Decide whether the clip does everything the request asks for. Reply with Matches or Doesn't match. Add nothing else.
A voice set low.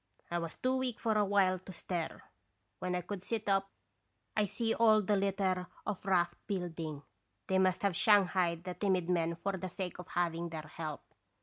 Doesn't match